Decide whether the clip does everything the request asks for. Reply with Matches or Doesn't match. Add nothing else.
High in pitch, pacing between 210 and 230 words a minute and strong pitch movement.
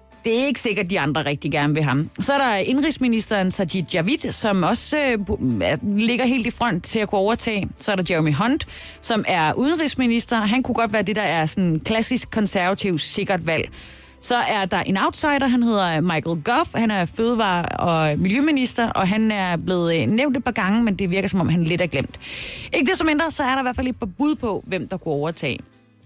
Matches